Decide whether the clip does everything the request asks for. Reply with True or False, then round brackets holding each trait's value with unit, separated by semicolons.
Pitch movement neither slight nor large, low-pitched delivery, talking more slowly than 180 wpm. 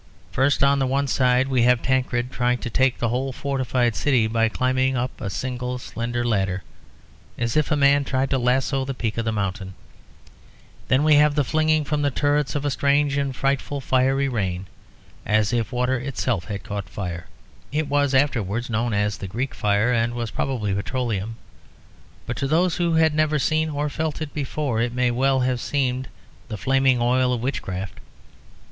False (3.2 semitones; 130 Hz; 185 wpm)